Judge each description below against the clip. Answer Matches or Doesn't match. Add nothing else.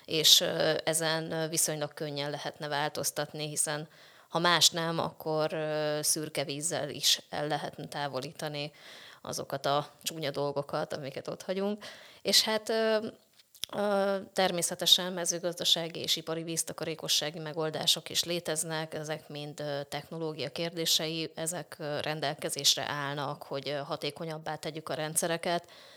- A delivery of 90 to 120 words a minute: Matches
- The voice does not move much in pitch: Matches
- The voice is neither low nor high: Matches